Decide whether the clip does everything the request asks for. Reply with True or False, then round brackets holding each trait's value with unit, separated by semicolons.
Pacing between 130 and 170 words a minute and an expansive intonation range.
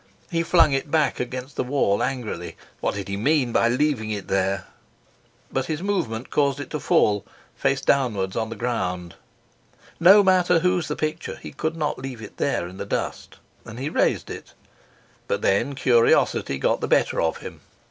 False (180 wpm; 6.8 semitones)